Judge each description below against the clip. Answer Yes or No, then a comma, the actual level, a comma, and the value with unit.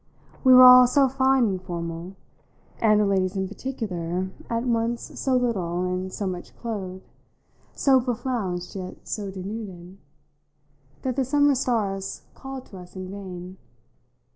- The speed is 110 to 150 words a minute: Yes, average, 140 wpm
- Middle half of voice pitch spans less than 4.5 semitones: No, wide, 5.4 semitones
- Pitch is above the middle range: Yes, high, 200 Hz